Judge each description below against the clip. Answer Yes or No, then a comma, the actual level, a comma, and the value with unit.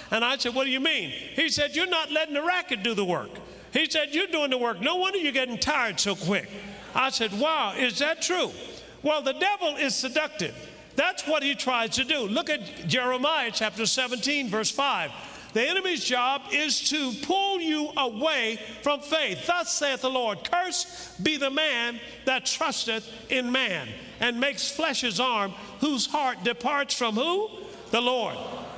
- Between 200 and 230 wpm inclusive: No, average, 185 wpm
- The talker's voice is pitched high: Yes, very high, 275 Hz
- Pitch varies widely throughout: No, average, 4.6 semitones